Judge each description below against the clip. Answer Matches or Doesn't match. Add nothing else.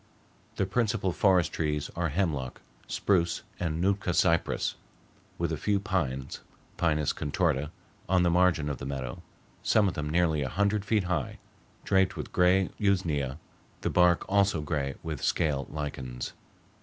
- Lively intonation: Doesn't match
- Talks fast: Doesn't match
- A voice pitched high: Doesn't match